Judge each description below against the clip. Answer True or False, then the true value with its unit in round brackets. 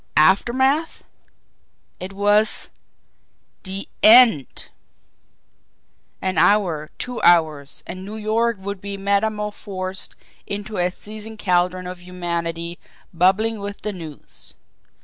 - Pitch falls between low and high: False (195 Hz)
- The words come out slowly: True (100 wpm)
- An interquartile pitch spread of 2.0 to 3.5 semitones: True (3.1 semitones)